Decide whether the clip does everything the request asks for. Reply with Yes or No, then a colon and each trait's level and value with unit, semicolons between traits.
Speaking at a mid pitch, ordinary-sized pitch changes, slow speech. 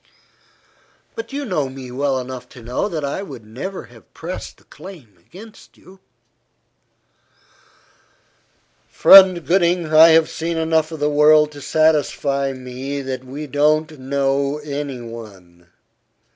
Yes: medium, 145 Hz; average, 3.7 semitones; slow, 130 wpm